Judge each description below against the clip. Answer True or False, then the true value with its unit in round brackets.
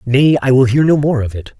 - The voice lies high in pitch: False (130 Hz)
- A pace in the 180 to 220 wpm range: False (300 wpm)